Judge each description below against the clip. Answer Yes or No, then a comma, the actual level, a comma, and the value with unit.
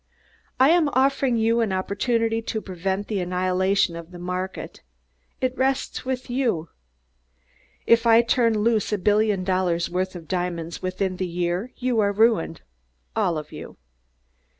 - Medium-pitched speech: No, high, 200 Hz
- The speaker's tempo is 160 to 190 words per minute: No, average, 150 wpm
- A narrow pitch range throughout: No, average, 4.2 semitones